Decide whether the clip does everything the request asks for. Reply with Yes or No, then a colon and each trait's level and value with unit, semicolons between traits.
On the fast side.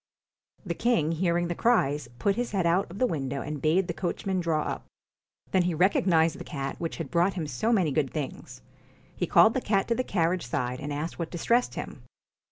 Yes: fast, 225 wpm